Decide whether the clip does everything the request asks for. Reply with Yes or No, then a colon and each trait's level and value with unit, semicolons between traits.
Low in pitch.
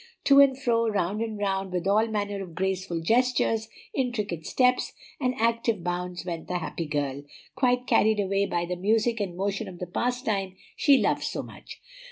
No: high, 205 Hz